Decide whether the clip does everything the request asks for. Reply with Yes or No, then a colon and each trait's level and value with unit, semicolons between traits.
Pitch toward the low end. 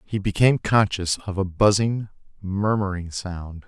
Yes: low, 100 Hz